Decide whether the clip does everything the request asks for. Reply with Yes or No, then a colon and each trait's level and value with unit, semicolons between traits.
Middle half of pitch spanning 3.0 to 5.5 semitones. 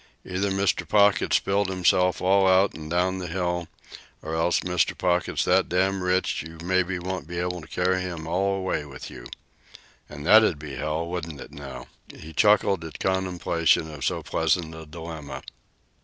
No: narrow, 2.6 semitones